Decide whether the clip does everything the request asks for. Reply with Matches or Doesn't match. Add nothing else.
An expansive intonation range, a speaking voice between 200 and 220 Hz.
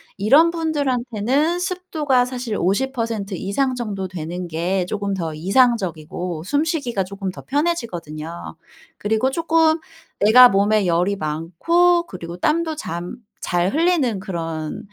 Matches